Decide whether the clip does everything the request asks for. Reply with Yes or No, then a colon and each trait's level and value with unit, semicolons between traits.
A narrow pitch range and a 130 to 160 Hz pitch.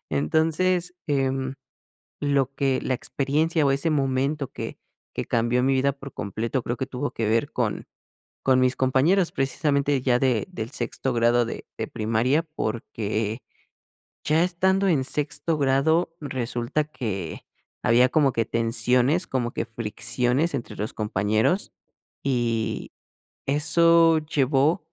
No: average, 4.4 semitones; low, 135 Hz